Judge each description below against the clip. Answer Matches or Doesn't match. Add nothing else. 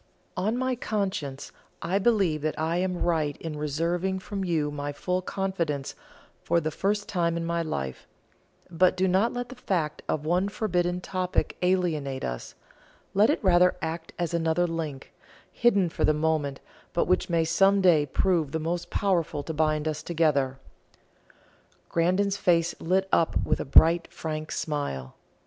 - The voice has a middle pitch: Matches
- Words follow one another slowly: Doesn't match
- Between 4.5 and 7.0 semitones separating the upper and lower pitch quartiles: Doesn't match